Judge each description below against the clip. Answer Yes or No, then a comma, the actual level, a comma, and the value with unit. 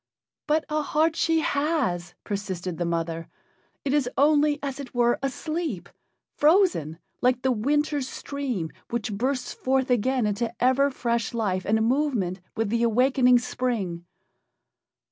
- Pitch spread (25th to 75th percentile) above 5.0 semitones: Yes, wide, 5.4 semitones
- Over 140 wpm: No, slow, 135 wpm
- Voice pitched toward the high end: Yes, very high, 250 Hz